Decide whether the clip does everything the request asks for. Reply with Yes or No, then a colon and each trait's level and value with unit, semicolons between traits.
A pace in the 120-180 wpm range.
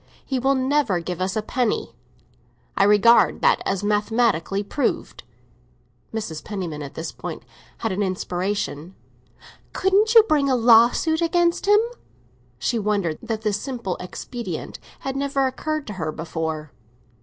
Yes: average, 140 wpm